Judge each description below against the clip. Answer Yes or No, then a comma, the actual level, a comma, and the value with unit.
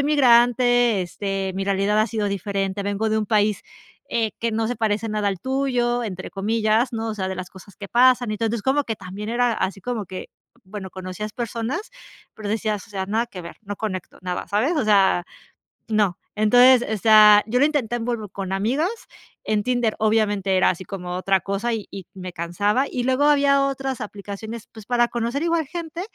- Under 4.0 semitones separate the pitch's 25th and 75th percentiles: Yes, average, 3.6 semitones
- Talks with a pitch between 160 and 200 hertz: No, high, 215 Hz